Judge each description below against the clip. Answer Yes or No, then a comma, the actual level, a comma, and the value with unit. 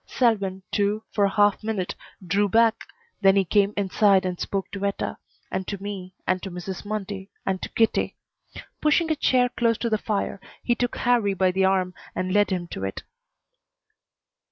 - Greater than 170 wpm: Yes, average, 180 wpm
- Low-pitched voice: No, high, 200 Hz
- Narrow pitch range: Yes, narrow, 2.3 semitones